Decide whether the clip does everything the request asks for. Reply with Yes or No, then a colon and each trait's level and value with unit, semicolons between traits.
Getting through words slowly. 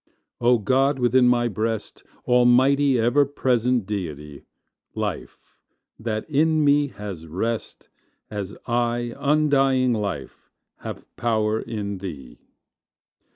Yes: slow, 105 wpm